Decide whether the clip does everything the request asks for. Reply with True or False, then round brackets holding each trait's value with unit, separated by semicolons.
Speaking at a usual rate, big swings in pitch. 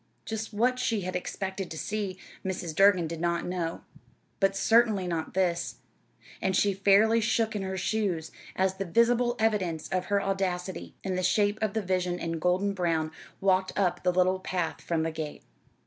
False (180 wpm; 2.5 semitones)